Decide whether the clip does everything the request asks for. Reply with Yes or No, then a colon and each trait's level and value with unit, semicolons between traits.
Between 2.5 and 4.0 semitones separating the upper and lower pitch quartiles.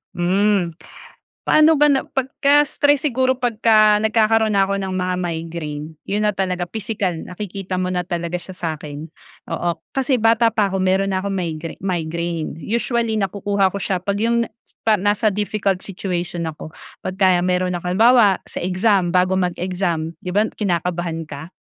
Yes: average, 3.5 semitones